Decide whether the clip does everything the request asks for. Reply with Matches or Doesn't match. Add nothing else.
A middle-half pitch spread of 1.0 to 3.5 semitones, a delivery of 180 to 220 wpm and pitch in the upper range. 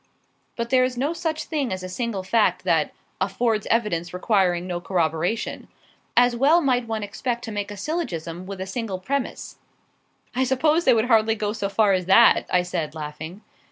Doesn't match